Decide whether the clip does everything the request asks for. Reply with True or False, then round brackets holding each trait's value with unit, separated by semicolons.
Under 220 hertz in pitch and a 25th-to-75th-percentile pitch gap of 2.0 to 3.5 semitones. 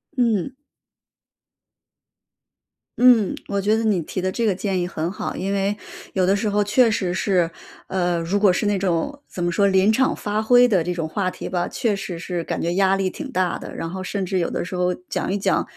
True (190 Hz; 2.6 semitones)